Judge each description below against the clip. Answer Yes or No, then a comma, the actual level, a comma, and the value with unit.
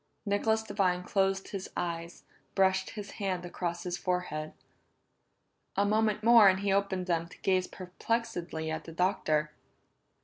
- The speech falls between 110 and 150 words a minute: Yes, average, 140 wpm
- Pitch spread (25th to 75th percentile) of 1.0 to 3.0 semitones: Yes, narrow, 2.5 semitones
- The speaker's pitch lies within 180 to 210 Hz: Yes, high, 190 Hz